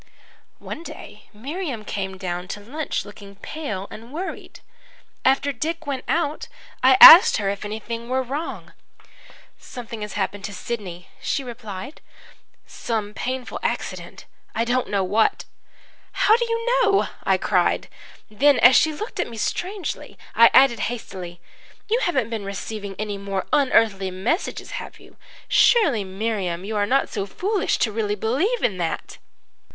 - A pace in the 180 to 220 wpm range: No, average, 150 wpm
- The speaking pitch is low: No, high, 230 Hz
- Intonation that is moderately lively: No, wide, 6.2 semitones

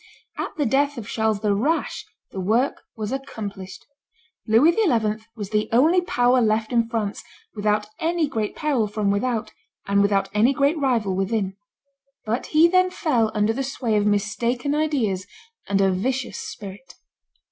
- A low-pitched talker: No, high, 225 Hz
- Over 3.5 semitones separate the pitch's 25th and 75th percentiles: Yes, average, 4.6 semitones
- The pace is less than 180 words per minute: Yes, average, 160 wpm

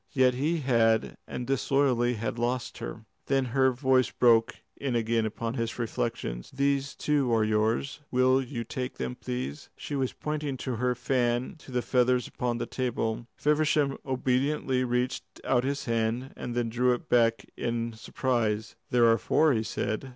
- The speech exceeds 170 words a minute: No, average, 165 wpm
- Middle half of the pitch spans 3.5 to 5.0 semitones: No, narrow, 2.4 semitones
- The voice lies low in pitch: Yes, low, 125 Hz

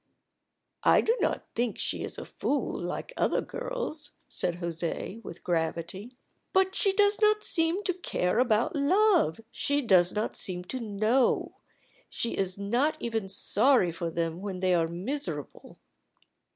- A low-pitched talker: No, high, 220 Hz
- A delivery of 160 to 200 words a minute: No, average, 150 wpm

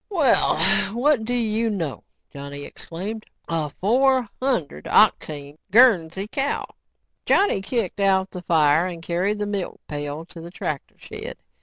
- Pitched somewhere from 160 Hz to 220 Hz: Yes, high, 190 Hz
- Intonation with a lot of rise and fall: Yes, wide, 6.1 semitones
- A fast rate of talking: No, average, 140 wpm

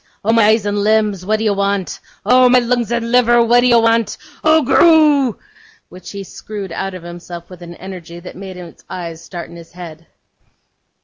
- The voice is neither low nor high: No, high, 205 Hz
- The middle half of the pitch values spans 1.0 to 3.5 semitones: No, average, 4.8 semitones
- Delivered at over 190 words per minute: Yes, average, 200 wpm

